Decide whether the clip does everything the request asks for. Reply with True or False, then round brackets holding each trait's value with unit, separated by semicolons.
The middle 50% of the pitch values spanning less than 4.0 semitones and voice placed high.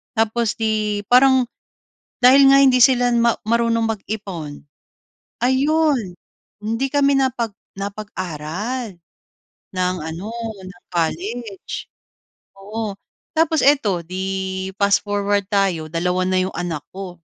False (4.7 semitones; 205 Hz)